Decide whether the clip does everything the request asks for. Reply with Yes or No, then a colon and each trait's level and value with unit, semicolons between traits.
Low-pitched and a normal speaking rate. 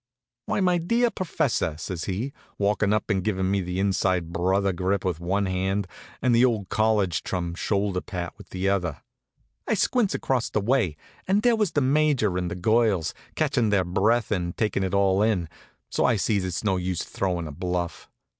Yes: low, 100 Hz; average, 190 wpm